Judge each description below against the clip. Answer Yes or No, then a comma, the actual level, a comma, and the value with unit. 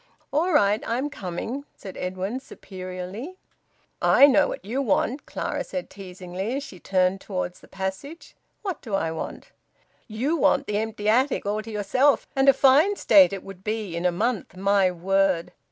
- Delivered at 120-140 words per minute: No, average, 175 wpm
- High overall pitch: Yes, high, 210 Hz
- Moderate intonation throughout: No, wide, 6.2 semitones